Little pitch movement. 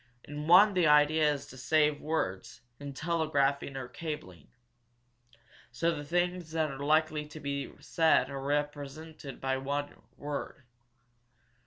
Yes: narrow, 2.2 semitones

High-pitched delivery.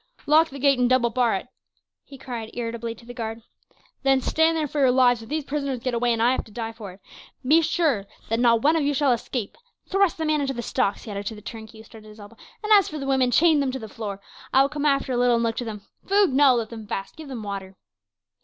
Yes: high, 245 Hz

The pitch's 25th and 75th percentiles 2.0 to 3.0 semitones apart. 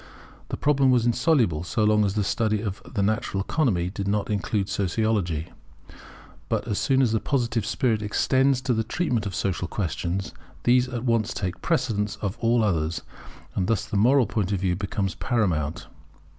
No: average, 3.7 semitones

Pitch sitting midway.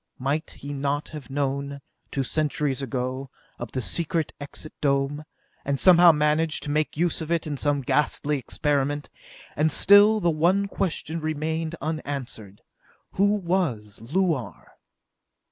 Yes: medium, 150 Hz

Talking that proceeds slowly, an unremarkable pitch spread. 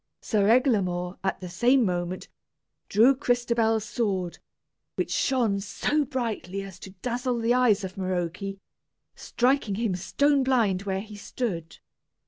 Yes: slow, 130 wpm; average, 4.6 semitones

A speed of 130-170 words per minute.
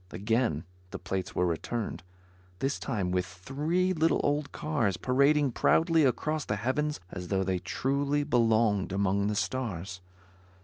Yes: average, 140 wpm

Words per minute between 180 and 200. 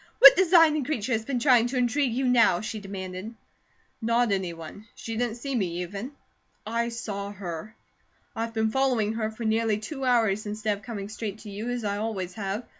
Yes: average, 190 wpm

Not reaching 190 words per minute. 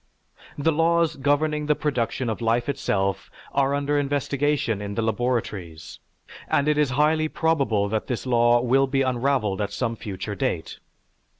Yes: average, 155 wpm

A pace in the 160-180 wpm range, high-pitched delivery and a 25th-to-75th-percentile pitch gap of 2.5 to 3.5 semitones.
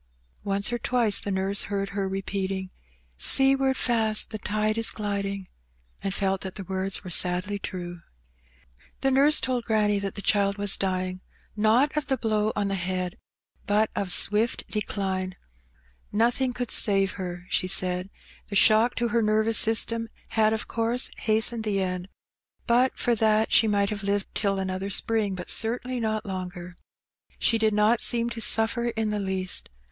Yes: average, 170 wpm; high, 205 Hz; average, 2.8 semitones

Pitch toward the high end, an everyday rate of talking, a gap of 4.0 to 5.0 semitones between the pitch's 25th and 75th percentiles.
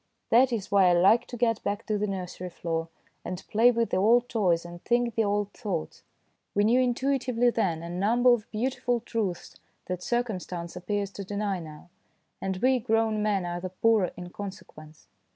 Yes: high, 205 Hz; average, 190 wpm; average, 4.4 semitones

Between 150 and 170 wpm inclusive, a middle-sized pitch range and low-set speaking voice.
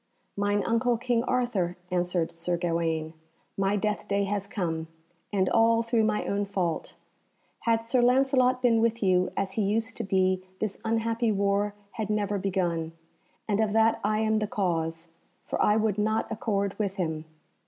No: average, 165 wpm; average, 3.4 semitones; high, 205 Hz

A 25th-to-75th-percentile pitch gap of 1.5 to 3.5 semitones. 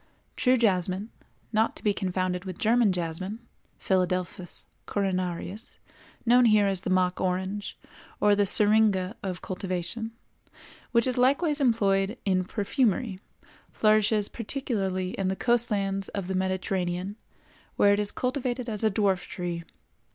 Yes: average, 3.2 semitones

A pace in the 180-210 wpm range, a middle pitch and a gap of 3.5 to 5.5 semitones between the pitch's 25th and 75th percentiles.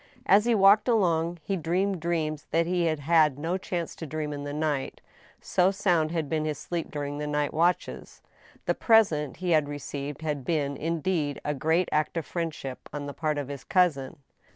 No: average, 195 wpm; medium, 160 Hz; average, 3.0 semitones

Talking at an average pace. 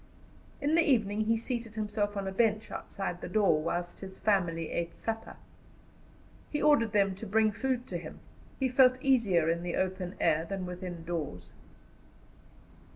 Yes: average, 160 wpm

